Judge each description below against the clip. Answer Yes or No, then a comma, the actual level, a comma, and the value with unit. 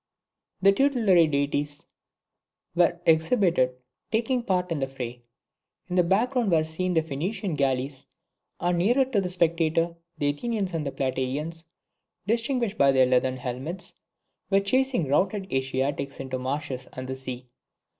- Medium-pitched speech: Yes, medium, 165 Hz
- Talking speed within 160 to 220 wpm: No, average, 145 wpm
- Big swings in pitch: Yes, wide, 6.4 semitones